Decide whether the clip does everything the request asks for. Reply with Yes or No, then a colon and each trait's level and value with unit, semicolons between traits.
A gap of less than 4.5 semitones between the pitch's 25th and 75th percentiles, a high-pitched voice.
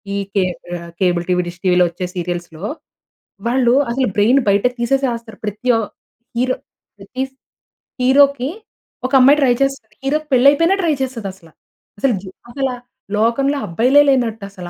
No: wide, 5.6 semitones; high, 235 Hz